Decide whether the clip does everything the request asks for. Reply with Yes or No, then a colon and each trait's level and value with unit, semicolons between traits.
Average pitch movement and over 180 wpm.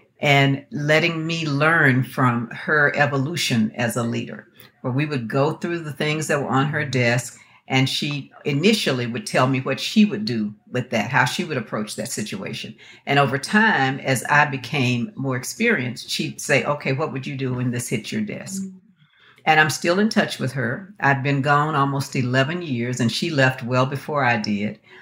Yes: average, 3.5 semitones; average, 190 wpm